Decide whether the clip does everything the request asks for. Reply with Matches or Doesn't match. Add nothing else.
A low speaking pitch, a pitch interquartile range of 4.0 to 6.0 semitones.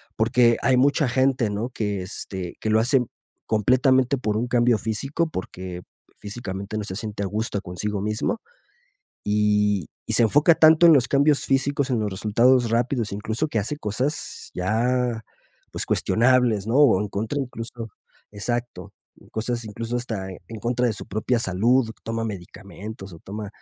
Doesn't match